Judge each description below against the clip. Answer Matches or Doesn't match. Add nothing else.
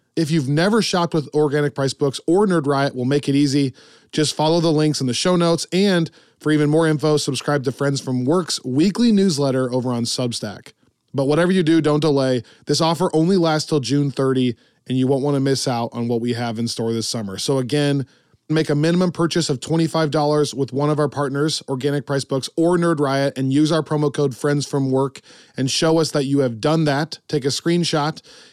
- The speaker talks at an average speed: Doesn't match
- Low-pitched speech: Doesn't match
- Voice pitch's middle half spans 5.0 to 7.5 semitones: Doesn't match